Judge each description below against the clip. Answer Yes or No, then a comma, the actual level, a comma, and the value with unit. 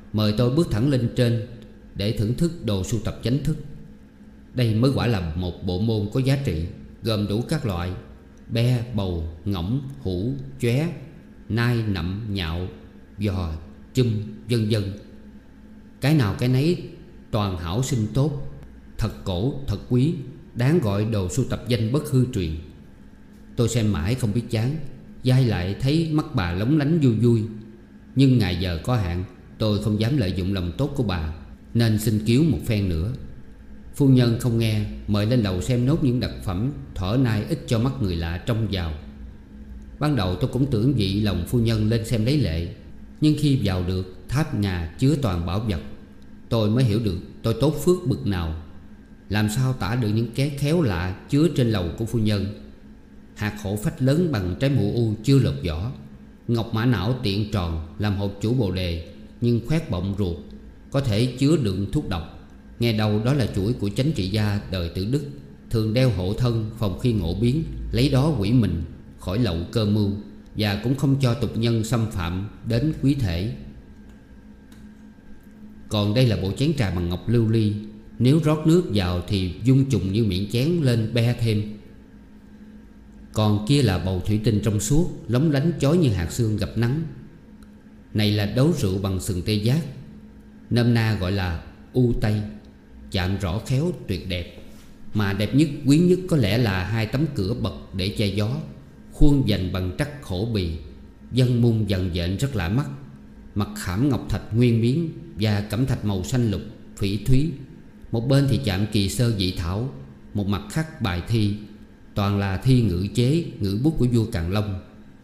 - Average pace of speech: Yes, average, 185 wpm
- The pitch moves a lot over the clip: No, average, 5.0 semitones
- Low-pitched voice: Yes, low, 110 Hz